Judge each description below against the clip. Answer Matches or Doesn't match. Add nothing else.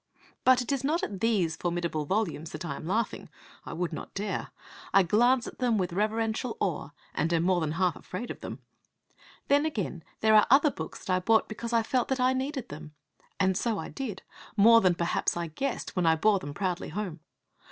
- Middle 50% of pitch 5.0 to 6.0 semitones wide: Matches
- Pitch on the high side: Matches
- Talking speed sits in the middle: Doesn't match